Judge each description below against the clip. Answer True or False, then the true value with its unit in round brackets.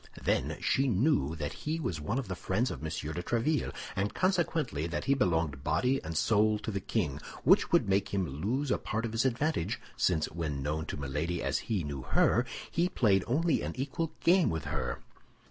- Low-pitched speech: True (100 Hz)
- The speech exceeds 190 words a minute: True (200 wpm)